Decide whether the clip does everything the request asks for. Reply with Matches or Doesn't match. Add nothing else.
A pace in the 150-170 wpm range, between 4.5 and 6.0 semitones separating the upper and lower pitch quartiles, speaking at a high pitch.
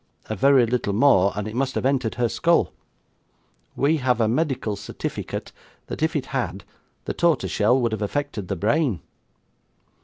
Doesn't match